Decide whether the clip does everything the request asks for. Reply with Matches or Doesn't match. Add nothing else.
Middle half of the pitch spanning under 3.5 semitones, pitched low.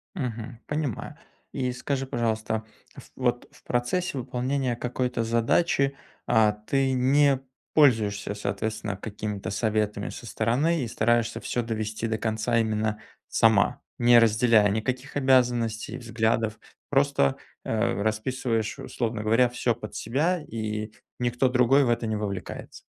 Matches